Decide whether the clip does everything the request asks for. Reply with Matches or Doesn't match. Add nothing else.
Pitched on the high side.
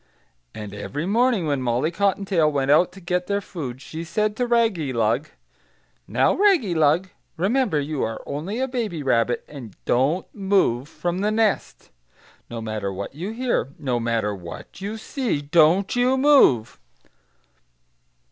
Doesn't match